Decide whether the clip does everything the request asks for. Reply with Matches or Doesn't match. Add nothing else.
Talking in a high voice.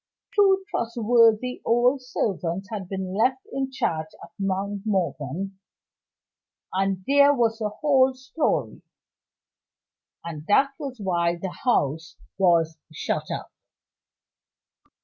Matches